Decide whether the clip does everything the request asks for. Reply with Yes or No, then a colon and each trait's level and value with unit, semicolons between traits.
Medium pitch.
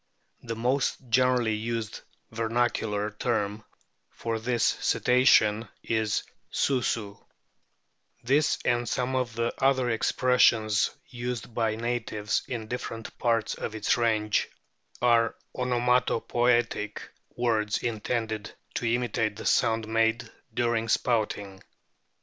No: low, 115 Hz